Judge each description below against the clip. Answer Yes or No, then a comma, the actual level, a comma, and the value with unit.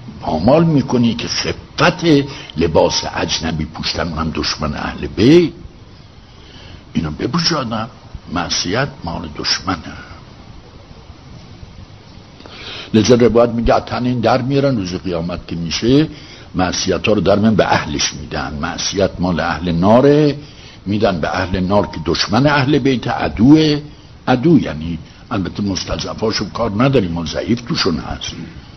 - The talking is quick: No, average, 120 wpm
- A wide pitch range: Yes, wide, 7.6 semitones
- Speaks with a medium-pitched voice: No, low, 105 Hz